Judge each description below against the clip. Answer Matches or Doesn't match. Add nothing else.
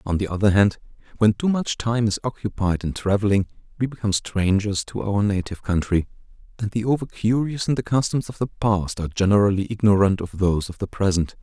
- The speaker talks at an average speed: Matches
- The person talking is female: Doesn't match